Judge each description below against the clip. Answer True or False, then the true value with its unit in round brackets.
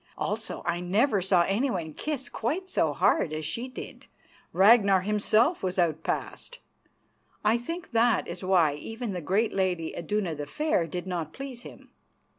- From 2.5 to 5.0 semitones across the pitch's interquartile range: False (5.6 semitones)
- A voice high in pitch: True (195 Hz)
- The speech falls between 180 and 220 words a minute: False (155 wpm)